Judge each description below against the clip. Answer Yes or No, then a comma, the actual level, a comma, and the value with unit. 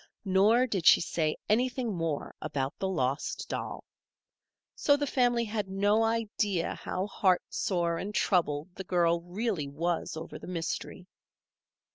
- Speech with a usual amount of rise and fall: Yes, average, 4.7 semitones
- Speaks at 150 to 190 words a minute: No, slow, 135 wpm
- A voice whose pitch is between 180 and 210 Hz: Yes, high, 190 Hz